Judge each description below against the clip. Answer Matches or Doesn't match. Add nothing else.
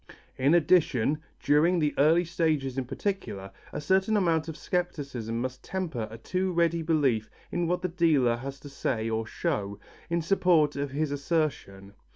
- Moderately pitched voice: Matches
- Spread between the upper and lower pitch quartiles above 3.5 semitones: Matches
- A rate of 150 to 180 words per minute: Matches